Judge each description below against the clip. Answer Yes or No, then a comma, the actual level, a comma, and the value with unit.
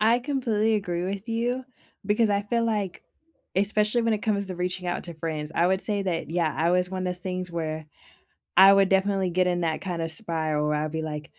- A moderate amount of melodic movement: Yes, average, 3.7 semitones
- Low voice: No, medium, 185 Hz